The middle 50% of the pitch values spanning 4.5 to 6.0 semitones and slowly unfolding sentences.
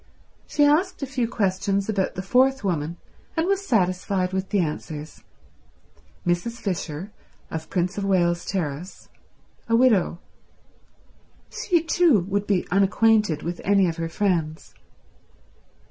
Yes: average, 4.8 semitones; slow, 130 wpm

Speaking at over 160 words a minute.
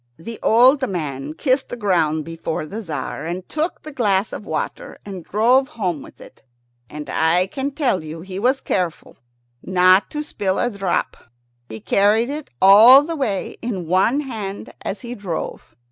Yes: average, 170 wpm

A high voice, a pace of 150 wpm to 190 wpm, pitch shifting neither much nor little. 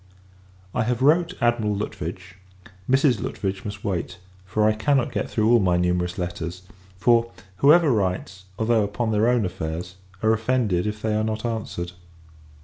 No: low, 105 Hz; average, 155 wpm; average, 4.5 semitones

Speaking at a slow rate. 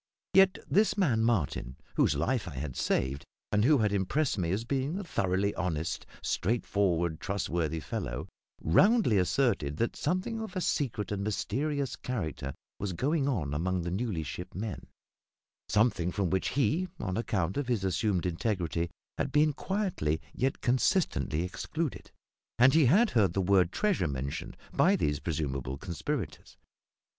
No: average, 150 wpm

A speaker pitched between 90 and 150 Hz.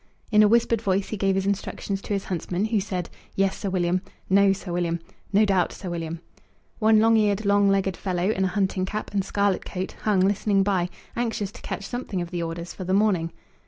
No: high, 195 Hz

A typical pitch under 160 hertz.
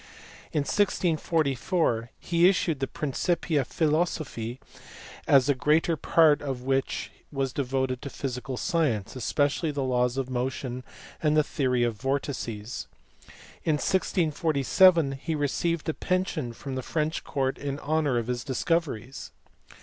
Yes: medium, 140 Hz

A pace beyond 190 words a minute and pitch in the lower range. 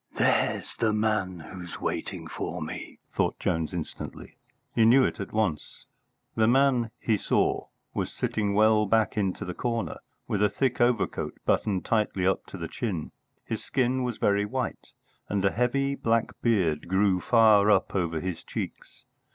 No: average, 160 wpm; low, 105 Hz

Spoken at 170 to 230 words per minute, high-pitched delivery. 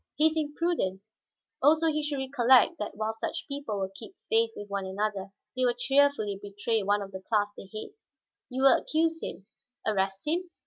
Yes: average, 185 wpm; high, 240 Hz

